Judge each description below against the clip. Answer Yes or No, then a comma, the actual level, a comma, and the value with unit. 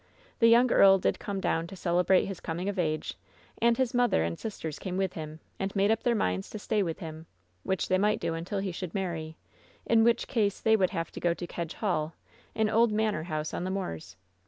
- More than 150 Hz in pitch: Yes, high, 190 Hz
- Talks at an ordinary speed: No, fast, 230 wpm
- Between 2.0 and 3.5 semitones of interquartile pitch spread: No, average, 4.5 semitones